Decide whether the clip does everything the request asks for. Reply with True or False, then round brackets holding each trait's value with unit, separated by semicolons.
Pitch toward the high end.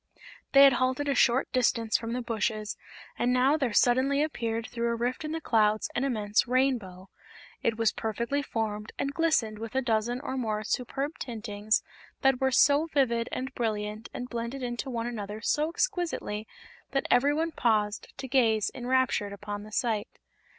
True (240 Hz)